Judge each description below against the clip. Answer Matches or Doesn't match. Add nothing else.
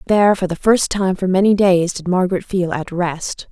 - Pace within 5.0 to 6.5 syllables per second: Matches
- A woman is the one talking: Matches